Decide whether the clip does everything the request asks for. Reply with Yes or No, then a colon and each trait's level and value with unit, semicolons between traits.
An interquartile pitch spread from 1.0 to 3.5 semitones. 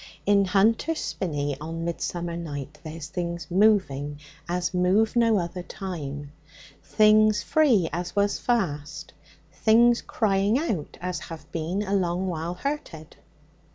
No: average, 4.4 semitones